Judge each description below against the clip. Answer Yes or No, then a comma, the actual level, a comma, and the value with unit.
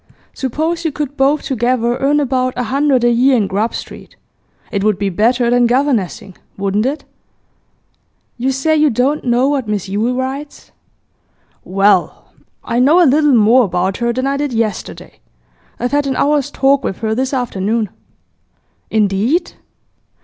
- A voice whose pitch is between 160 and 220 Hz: No, very high, 250 Hz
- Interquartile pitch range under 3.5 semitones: No, average, 4.2 semitones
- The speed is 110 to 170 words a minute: Yes, average, 155 wpm